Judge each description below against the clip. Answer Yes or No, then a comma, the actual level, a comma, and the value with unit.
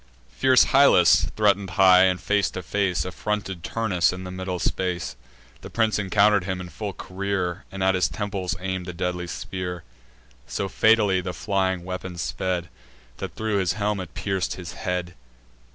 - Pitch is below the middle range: Yes, very low, 95 Hz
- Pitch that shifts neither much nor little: No, narrow, 2.0 semitones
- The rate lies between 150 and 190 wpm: Yes, average, 170 wpm